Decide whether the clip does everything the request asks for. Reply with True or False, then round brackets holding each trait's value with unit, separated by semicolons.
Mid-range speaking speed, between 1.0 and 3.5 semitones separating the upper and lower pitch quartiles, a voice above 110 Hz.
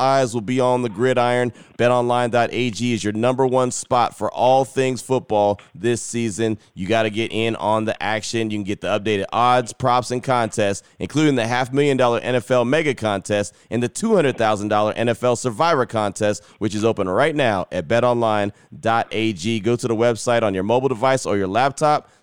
True (190 wpm; 2.6 semitones; 120 Hz)